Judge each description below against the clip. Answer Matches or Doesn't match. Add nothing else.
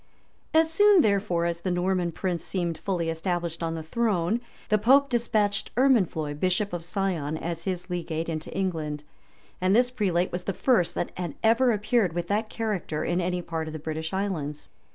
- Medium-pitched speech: Matches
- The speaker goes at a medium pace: Matches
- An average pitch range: Matches